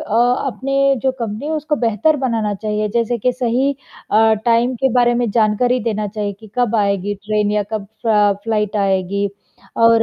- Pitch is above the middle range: Yes, high, 225 Hz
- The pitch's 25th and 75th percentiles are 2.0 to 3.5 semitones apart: Yes, average, 2.8 semitones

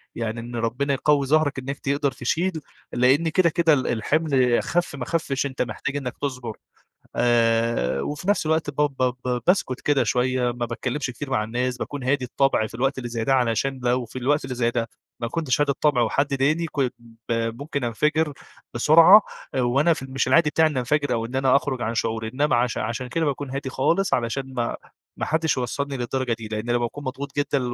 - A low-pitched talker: Yes, low, 130 Hz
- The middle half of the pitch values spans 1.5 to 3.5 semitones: Yes, average, 3.2 semitones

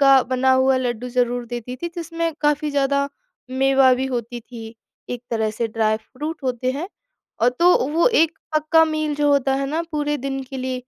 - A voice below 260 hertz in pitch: No, very high, 265 Hz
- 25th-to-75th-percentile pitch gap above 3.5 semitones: No, average, 3.2 semitones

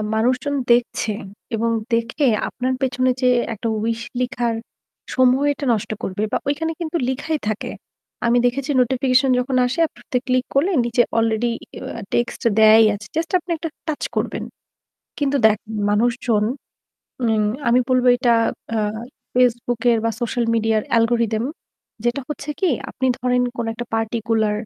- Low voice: No, high, 245 Hz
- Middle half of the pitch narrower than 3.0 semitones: Yes, narrow, 2.5 semitones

